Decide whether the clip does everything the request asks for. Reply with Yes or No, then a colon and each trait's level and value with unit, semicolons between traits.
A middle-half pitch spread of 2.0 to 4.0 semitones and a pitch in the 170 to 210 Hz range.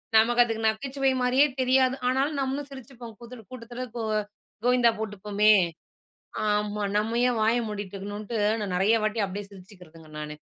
No: average, 3.4 semitones; high, 225 Hz